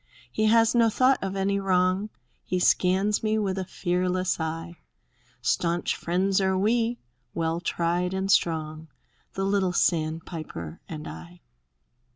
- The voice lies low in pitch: No, medium, 185 Hz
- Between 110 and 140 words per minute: Yes, slow, 135 wpm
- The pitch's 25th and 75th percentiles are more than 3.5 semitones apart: No, average, 2.9 semitones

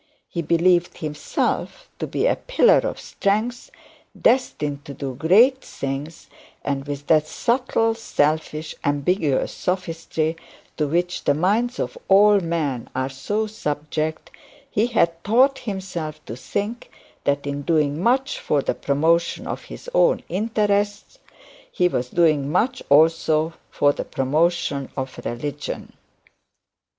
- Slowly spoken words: Yes, slow, 130 wpm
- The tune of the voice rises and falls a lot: Yes, wide, 6.0 semitones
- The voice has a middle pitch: Yes, medium, 165 Hz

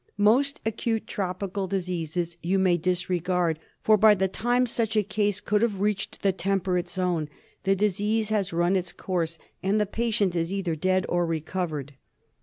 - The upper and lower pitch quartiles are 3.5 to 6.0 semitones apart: No, average, 3.0 semitones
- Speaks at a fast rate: No, average, 165 wpm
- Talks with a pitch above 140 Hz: Yes, high, 190 Hz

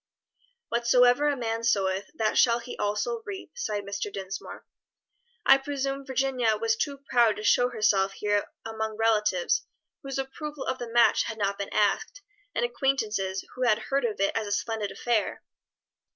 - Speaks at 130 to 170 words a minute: Yes, average, 165 wpm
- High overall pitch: Yes, high, 230 Hz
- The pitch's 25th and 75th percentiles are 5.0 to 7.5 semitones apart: No, average, 4.3 semitones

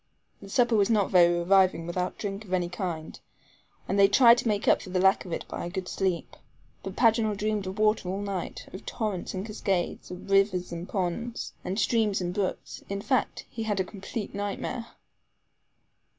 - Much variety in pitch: No, average, 2.7 semitones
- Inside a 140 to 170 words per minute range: No, average, 195 wpm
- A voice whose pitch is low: No, high, 195 Hz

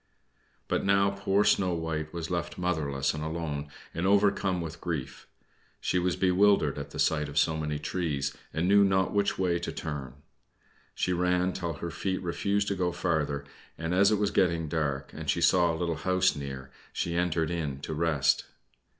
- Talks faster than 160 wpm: Yes, average, 185 wpm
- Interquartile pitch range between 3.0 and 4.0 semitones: Yes, average, 3.4 semitones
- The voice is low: Yes, very low, 85 Hz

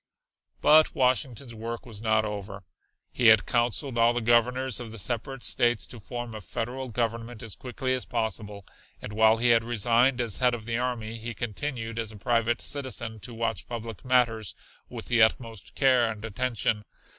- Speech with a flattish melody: Yes, narrow, 1.9 semitones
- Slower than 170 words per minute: No, average, 180 wpm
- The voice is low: Yes, low, 115 Hz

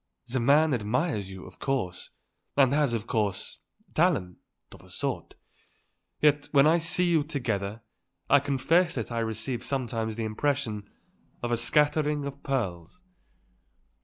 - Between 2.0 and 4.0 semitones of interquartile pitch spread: No, average, 5.0 semitones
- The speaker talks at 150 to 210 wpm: No, average, 140 wpm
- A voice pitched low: Yes, low, 130 Hz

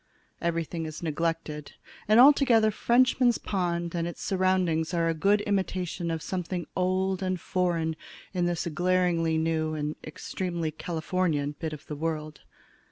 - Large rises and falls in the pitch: No, narrow, 2.6 semitones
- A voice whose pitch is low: No, medium, 170 Hz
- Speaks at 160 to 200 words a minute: No, average, 140 wpm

